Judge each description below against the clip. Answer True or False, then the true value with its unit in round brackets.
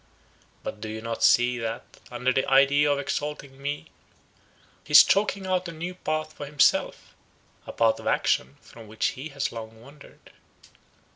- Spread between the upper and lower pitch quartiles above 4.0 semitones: True (4.6 semitones)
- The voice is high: False (135 Hz)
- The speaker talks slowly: False (165 wpm)